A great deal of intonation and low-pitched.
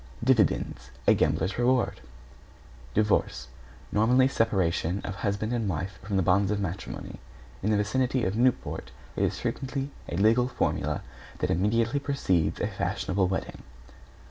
No: average, 4.6 semitones; low, 105 Hz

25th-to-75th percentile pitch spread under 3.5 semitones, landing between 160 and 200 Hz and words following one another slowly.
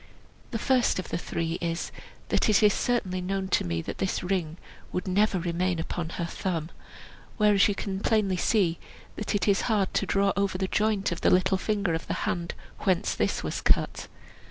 No: average, 2.8 semitones; high, 190 Hz; average, 200 wpm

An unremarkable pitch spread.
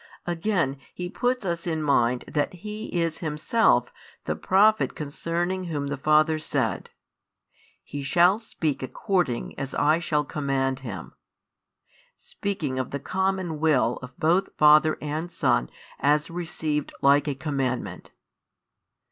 Yes: average, 3.9 semitones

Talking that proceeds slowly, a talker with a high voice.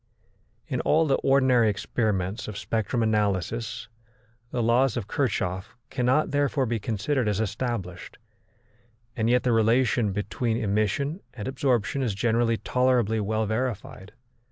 No: slow, 130 wpm; low, 115 Hz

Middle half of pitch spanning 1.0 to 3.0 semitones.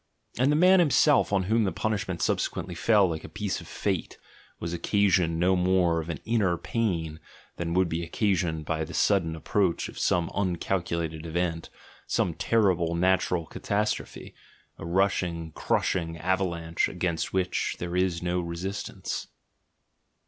Yes: average, 2.7 semitones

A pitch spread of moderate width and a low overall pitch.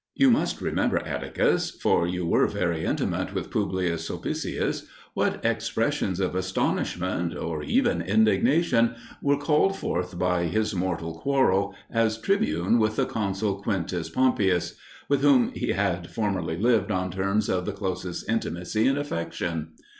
Yes: average, 4.6 semitones; very low, 95 Hz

